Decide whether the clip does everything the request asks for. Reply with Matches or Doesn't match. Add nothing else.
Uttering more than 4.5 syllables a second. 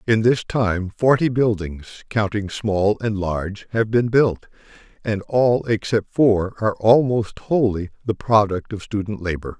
Doesn't match